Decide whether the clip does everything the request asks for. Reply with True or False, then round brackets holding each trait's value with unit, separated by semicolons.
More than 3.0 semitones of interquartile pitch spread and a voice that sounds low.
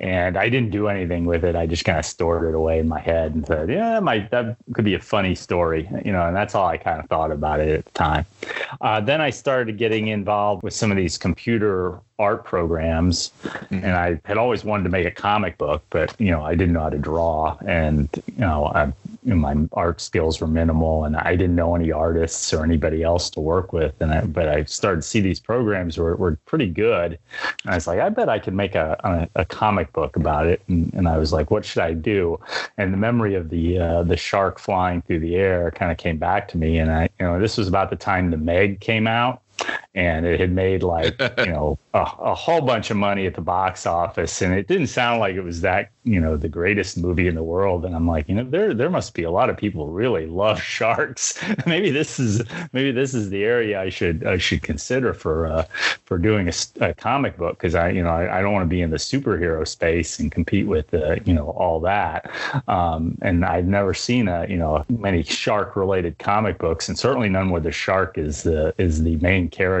True (3.7 semitones; 90 Hz)